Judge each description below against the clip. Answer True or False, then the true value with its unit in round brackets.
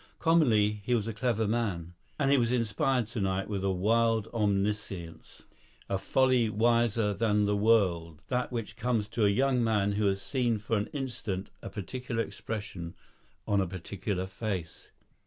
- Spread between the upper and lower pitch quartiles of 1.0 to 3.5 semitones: True (2.9 semitones)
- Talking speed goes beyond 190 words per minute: False (160 wpm)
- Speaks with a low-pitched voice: True (105 Hz)